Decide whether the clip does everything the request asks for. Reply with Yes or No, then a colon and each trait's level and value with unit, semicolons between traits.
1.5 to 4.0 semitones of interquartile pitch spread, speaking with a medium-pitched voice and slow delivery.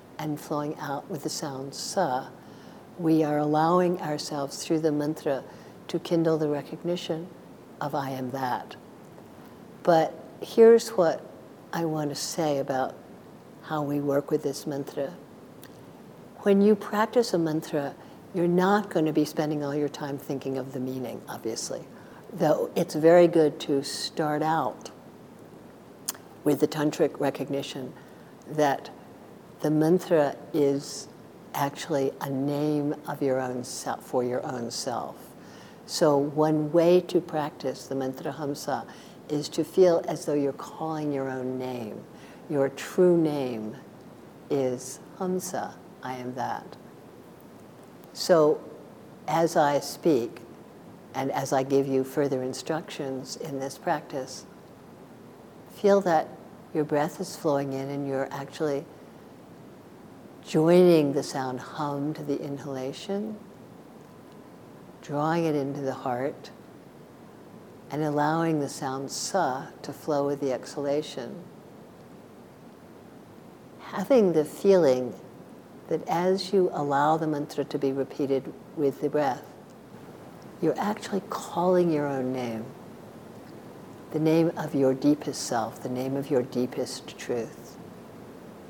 Yes: average, 3.1 semitones; medium, 150 Hz; slow, 125 wpm